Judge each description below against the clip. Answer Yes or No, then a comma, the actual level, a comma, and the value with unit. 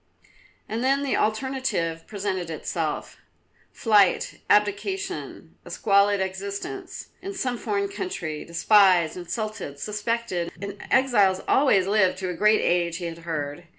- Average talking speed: No, slow, 125 wpm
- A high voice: Yes, high, 200 Hz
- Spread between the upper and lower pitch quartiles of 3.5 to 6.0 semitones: Yes, average, 5.0 semitones